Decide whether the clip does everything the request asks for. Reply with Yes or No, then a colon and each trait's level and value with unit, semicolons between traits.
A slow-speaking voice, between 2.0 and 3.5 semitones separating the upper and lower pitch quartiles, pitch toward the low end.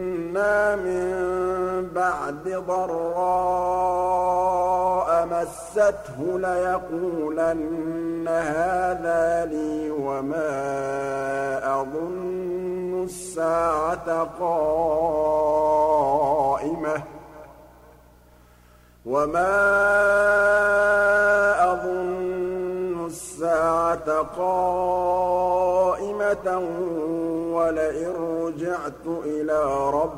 No: slow, 40 wpm; narrow, 2.5 semitones; medium, 175 Hz